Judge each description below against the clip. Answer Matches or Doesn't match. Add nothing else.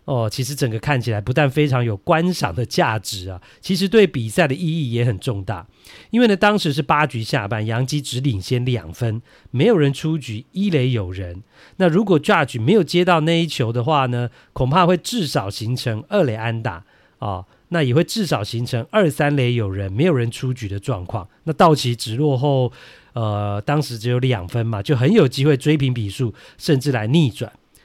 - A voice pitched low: Matches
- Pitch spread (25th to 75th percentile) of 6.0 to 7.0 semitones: Doesn't match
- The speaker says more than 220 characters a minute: Matches